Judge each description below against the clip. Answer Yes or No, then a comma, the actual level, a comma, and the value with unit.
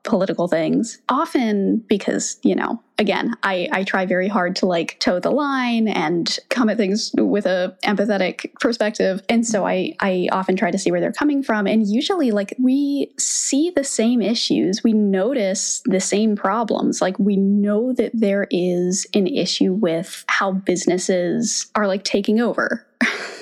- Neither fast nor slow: Yes, average, 165 wpm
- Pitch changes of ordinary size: Yes, average, 4.3 semitones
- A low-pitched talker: No, high, 210 Hz